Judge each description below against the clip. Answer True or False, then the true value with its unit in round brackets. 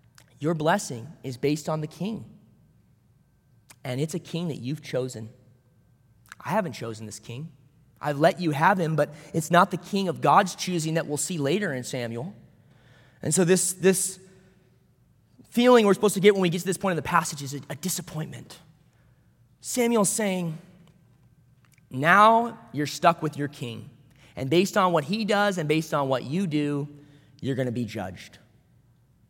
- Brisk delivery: False (175 wpm)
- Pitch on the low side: False (150 Hz)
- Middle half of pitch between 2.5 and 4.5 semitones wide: False (5.6 semitones)